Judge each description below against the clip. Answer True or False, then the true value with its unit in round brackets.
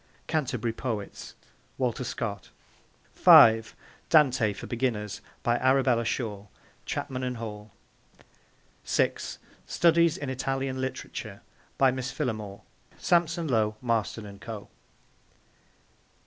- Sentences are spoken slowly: True (100 wpm)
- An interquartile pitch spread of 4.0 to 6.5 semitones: False (3.6 semitones)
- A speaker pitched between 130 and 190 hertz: False (120 Hz)